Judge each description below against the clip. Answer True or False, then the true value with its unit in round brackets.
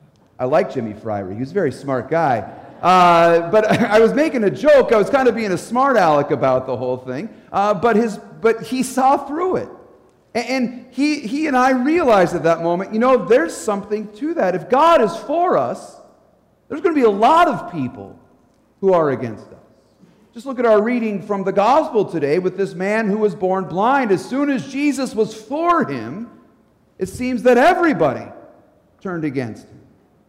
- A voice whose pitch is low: False (215 Hz)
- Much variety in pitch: True (6.6 semitones)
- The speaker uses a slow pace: False (195 wpm)